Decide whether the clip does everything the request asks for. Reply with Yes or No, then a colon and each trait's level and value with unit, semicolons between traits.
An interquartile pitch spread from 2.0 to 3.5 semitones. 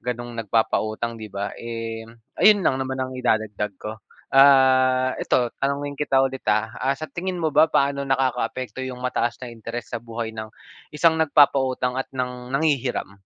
Yes: average, 3.0 semitones